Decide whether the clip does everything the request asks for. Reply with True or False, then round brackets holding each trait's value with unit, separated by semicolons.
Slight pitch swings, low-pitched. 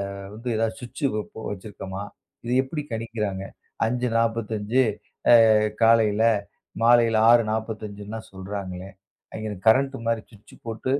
True (1.9 semitones; 110 Hz)